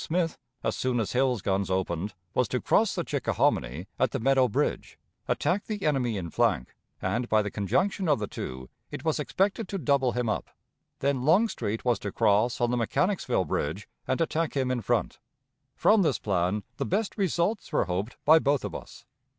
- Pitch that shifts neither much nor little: No, wide, 7.5 semitones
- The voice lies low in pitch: Yes, low, 125 Hz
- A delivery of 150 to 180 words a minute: No, average, 190 wpm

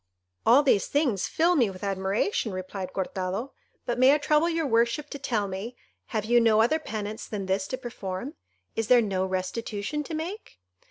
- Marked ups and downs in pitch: Yes, wide, 6.4 semitones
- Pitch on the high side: Yes, high, 225 Hz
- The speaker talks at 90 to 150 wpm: No, average, 180 wpm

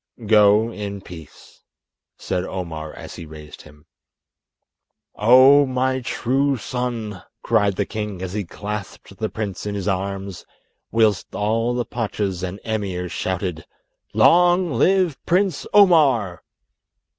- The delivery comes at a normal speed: No, slow, 120 wpm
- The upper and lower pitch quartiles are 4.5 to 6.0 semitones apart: Yes, average, 4.9 semitones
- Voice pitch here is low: Yes, low, 105 Hz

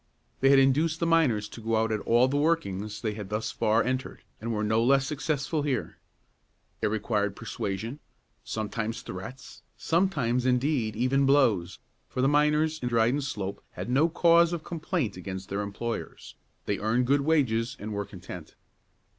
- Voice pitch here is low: Yes, low, 120 Hz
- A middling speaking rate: Yes, average, 165 wpm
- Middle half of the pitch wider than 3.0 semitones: Yes, average, 5.2 semitones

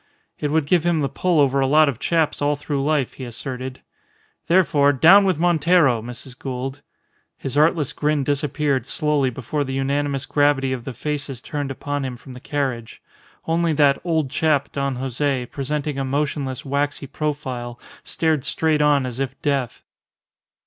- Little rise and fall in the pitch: Yes, narrow, 2.3 semitones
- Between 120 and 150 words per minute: No, average, 165 wpm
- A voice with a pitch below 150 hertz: Yes, medium, 140 Hz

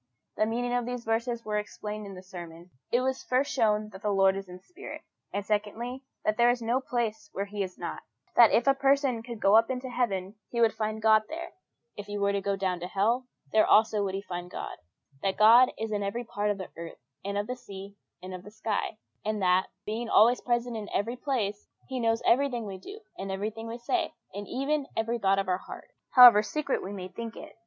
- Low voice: No, high, 215 Hz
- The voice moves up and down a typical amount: Yes, average, 3.5 semitones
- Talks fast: Yes, fast, 230 wpm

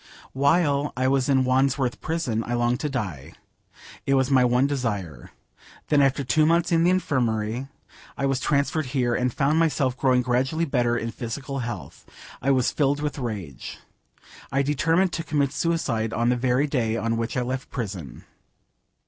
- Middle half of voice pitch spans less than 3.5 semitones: Yes, average, 3.1 semitones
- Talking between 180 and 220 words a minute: No, average, 170 wpm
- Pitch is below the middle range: Yes, low, 130 Hz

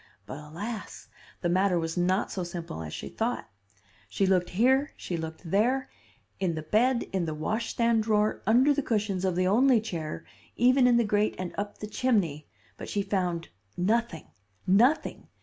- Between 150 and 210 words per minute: Yes, average, 170 wpm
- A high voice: Yes, high, 200 Hz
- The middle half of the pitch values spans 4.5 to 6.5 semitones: Yes, average, 5.0 semitones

